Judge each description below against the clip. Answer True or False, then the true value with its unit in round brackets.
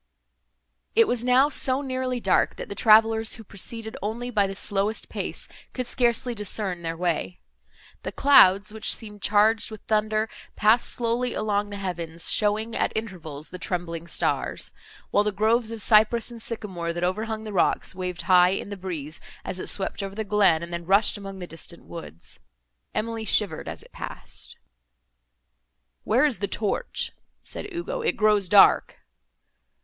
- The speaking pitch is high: True (210 Hz)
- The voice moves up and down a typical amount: True (3.6 semitones)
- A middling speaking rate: True (165 wpm)